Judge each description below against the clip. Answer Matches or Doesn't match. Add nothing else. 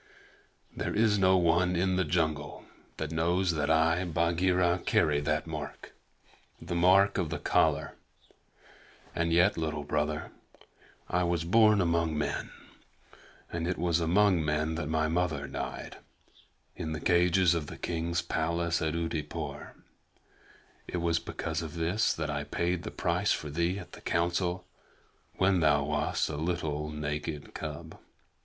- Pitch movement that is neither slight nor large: Doesn't match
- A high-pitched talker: Doesn't match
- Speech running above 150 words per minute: Doesn't match